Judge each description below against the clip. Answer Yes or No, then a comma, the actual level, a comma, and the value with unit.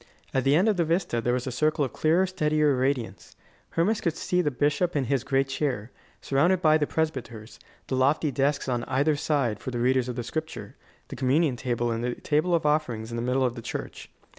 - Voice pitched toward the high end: No, medium, 140 Hz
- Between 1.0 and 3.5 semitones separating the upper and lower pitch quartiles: No, average, 3.9 semitones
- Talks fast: Yes, fast, 220 wpm